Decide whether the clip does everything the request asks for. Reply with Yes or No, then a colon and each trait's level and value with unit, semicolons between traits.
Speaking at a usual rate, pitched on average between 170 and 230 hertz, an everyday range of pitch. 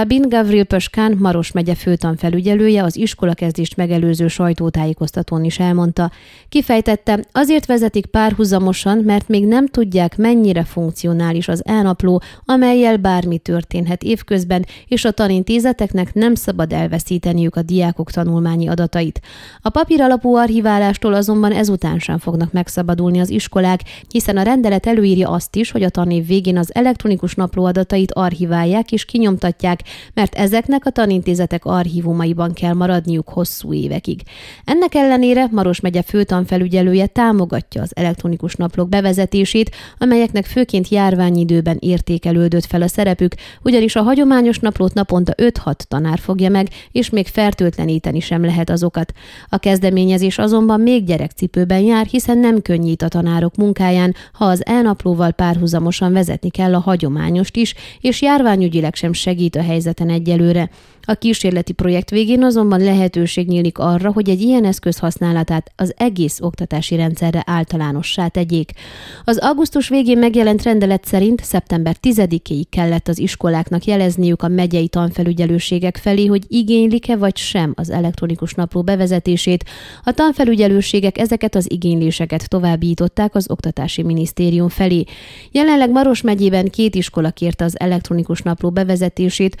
Yes: average, 130 wpm; medium, 185 Hz; average, 3.8 semitones